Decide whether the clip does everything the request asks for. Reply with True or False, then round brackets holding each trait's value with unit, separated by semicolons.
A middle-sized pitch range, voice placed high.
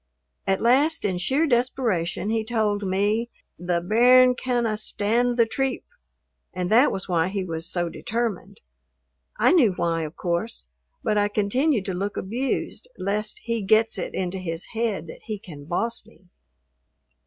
True (4.3 semitones; 210 Hz)